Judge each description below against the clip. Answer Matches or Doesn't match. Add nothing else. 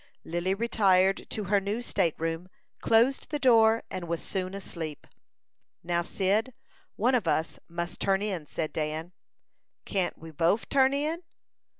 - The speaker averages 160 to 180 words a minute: Doesn't match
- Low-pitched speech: Doesn't match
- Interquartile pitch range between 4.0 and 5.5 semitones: Matches